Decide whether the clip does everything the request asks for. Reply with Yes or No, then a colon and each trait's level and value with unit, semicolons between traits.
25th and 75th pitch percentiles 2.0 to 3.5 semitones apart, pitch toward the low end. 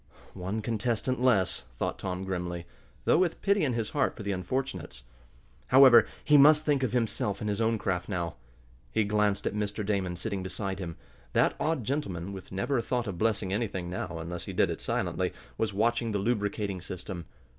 No: average, 4.2 semitones; low, 105 Hz